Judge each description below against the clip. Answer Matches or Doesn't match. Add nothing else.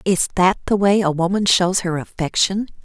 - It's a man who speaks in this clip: Doesn't match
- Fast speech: Doesn't match